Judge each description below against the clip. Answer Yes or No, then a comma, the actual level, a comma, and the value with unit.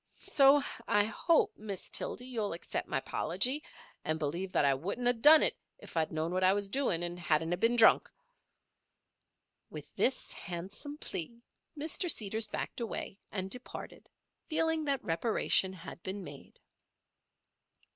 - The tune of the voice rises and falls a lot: Yes, wide, 6.3 semitones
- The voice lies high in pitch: Yes, high, 200 Hz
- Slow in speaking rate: No, average, 150 wpm